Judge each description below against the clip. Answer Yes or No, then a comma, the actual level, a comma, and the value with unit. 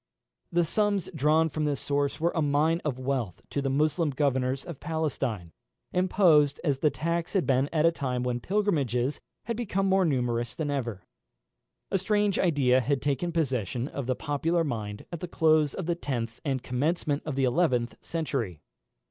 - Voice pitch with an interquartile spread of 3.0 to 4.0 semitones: No, average, 4.5 semitones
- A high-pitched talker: No, medium, 145 Hz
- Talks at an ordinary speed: Yes, average, 175 wpm